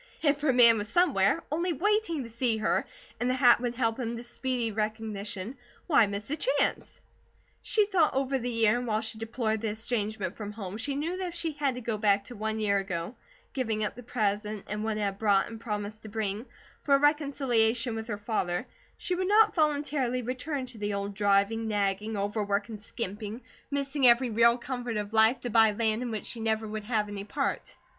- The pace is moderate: No, fast, 210 wpm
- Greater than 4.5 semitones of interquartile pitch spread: No, average, 3.6 semitones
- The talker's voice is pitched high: Yes, high, 225 Hz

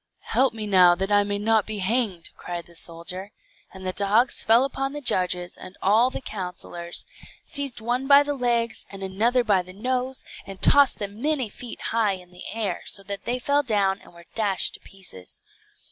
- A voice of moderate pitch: No, high, 205 Hz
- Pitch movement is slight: No, average, 4.7 semitones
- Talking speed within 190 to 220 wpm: Yes, average, 195 wpm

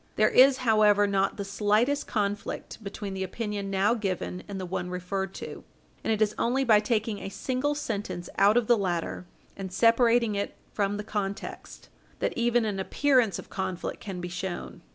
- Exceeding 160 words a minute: Yes, average, 180 wpm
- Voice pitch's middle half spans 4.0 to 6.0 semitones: No, average, 3.0 semitones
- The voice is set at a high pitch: Yes, high, 205 Hz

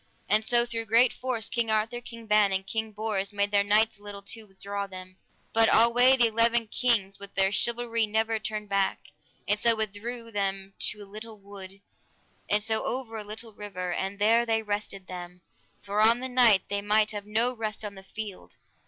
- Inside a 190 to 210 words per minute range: Yes, average, 195 wpm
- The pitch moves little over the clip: Yes, narrow, 2.2 semitones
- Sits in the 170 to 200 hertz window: No, high, 215 Hz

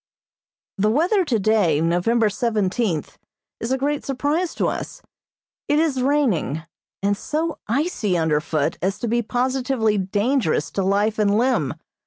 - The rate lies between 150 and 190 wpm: No, slow, 135 wpm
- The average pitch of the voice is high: Yes, high, 225 Hz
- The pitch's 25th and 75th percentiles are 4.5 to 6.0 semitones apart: Yes, wide, 5.6 semitones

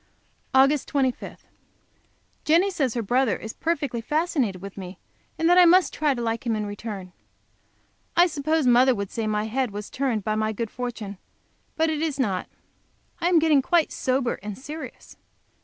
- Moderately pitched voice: No, very high, 255 Hz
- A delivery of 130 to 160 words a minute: No, average, 175 wpm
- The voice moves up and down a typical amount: No, wide, 6.2 semitones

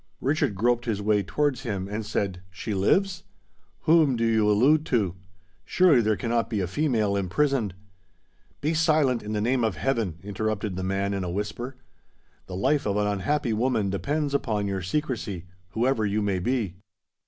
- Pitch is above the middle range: No, low, 110 Hz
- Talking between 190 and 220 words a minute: No, average, 165 wpm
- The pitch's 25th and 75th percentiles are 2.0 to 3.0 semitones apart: No, average, 5.0 semitones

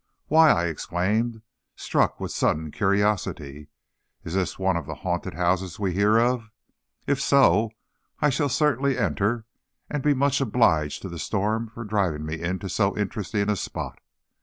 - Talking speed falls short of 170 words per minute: Yes, average, 160 wpm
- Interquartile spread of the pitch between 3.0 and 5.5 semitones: Yes, average, 5.2 semitones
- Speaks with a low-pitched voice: Yes, low, 100 Hz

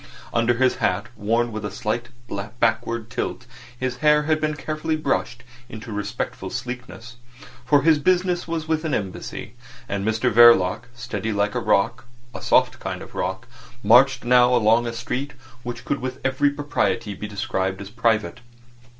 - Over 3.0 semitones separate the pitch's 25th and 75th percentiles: Yes, average, 3.5 semitones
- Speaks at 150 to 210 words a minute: Yes, average, 155 wpm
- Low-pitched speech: Yes, low, 120 Hz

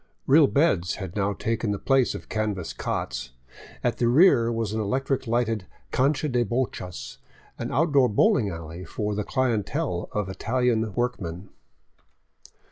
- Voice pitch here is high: No, low, 115 Hz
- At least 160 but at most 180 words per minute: No, average, 140 wpm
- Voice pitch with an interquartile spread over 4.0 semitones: Yes, average, 4.6 semitones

